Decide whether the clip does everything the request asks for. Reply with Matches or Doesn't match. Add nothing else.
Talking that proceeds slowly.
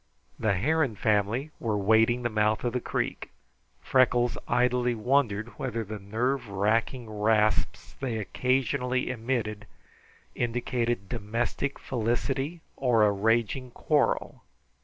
Matches